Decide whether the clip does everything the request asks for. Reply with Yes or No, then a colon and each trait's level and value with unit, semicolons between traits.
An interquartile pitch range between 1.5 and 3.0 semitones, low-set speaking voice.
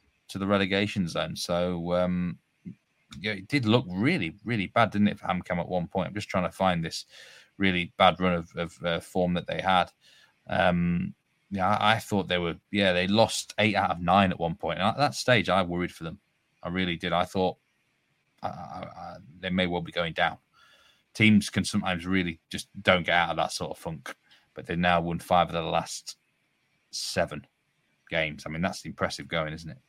Yes: narrow, 2.5 semitones; very low, 90 Hz